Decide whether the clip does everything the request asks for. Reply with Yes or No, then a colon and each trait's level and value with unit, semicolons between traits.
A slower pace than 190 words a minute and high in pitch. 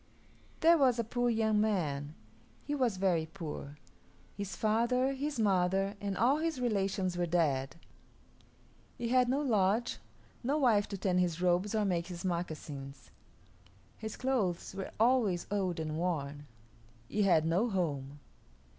Yes: average, 145 wpm; high, 195 Hz